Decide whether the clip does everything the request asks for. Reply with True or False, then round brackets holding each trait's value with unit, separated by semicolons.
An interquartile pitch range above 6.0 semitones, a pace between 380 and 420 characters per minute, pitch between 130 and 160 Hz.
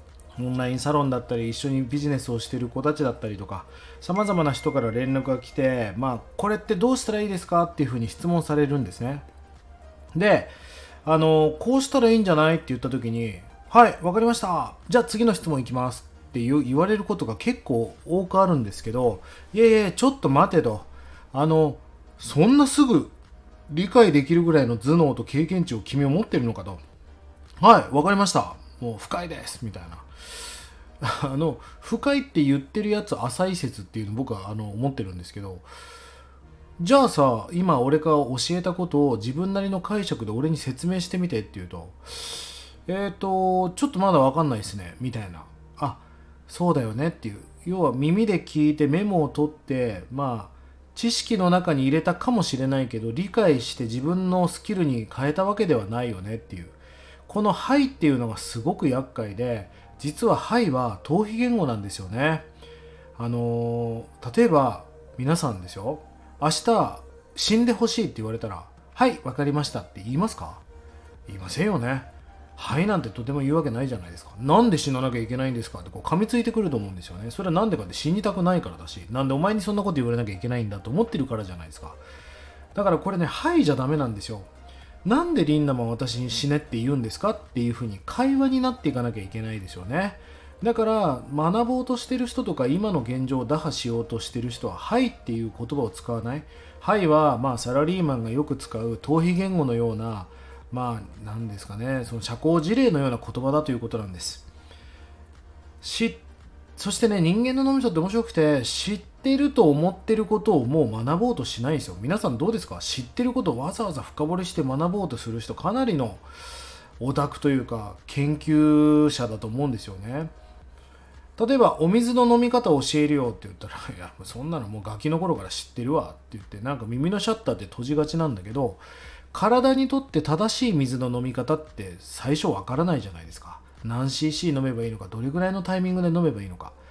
True (8.0 semitones; 390 characters per minute; 135 Hz)